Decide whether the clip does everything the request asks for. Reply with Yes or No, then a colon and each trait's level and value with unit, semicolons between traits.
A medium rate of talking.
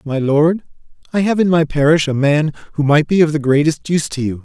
No: fast, 245 wpm